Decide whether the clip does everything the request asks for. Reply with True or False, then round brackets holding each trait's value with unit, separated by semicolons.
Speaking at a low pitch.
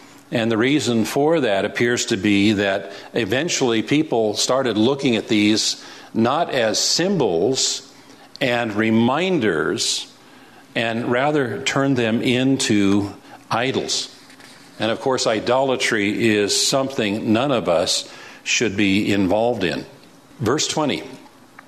True (115 Hz)